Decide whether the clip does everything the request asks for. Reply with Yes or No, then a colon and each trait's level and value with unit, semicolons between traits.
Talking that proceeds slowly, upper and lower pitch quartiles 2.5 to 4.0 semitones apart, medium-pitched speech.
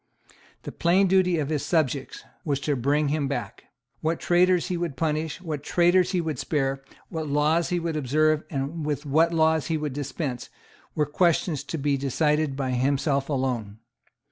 No: average, 175 wpm; average, 3.1 semitones; medium, 150 Hz